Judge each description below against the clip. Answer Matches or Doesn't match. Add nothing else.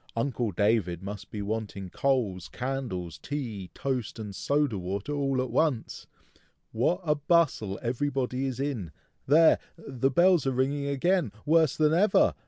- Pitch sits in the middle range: Doesn't match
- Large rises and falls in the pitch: Matches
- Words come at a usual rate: Matches